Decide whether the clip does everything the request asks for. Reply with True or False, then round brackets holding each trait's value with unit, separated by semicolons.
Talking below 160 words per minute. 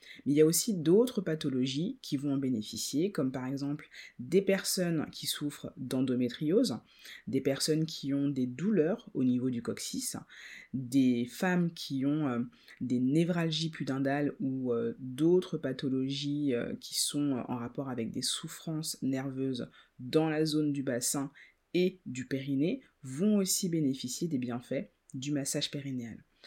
True (145 wpm)